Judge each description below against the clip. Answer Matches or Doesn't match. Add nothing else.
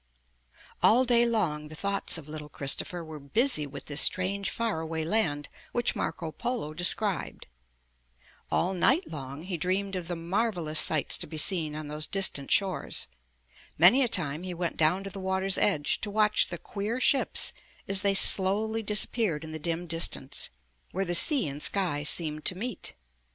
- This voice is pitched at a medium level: Matches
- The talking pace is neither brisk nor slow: Matches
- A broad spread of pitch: Doesn't match